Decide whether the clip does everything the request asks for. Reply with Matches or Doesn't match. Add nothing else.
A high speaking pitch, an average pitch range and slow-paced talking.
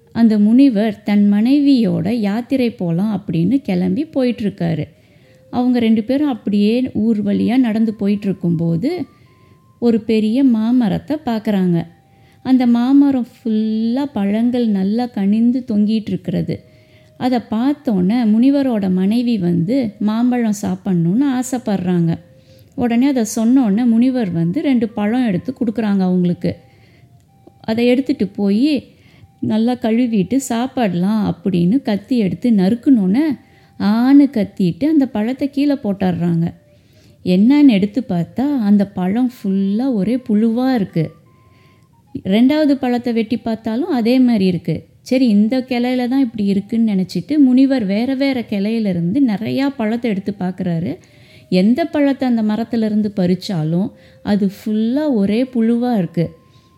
Matches